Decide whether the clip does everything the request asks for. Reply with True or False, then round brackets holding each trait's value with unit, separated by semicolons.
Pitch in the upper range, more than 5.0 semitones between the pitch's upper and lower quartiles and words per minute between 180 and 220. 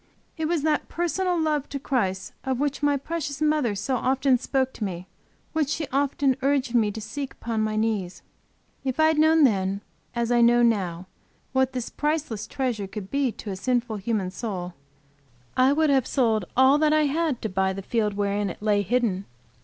True (250 Hz; 5.5 semitones; 190 wpm)